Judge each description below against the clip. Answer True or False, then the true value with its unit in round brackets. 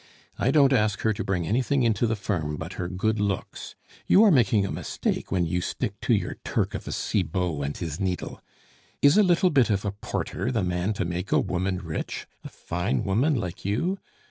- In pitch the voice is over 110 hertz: False (100 Hz)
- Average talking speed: False (210 wpm)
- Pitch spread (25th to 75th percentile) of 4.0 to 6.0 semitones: True (5.0 semitones)